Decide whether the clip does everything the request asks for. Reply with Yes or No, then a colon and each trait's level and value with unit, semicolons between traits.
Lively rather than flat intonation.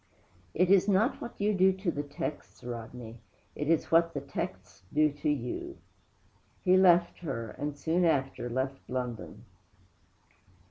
Yes: wide, 5.7 semitones